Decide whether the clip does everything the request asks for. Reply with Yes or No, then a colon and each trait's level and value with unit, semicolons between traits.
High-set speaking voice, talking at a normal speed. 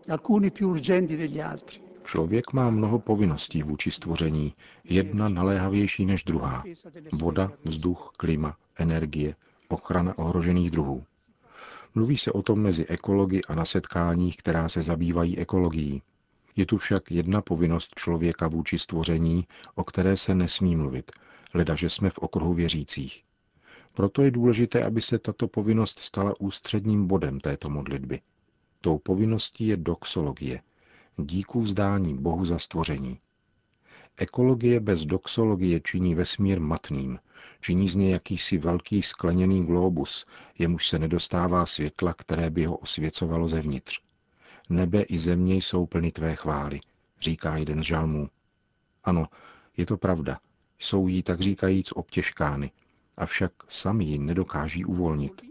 No: very low, 90 Hz; average, 125 wpm